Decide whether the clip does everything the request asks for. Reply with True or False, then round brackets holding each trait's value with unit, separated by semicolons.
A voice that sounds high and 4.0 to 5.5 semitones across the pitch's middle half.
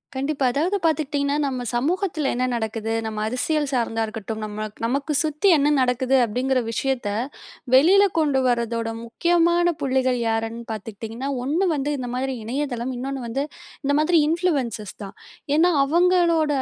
True (265 Hz; 4.7 semitones)